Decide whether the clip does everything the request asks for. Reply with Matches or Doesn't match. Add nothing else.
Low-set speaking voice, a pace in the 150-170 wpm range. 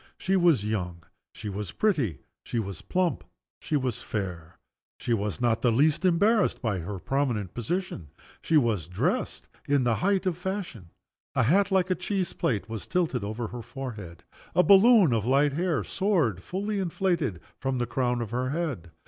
Doesn't match